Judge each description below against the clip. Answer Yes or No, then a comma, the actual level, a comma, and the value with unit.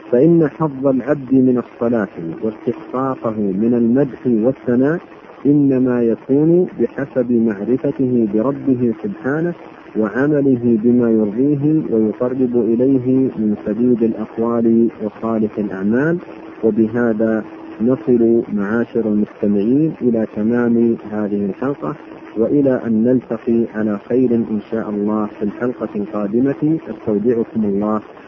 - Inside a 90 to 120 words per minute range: Yes, average, 100 wpm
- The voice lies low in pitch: Yes, low, 115 Hz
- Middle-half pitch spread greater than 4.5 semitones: No, average, 3.2 semitones